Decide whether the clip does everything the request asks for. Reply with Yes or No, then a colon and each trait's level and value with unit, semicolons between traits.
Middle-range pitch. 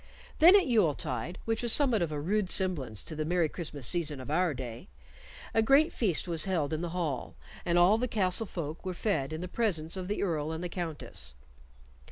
Yes: medium, 175 Hz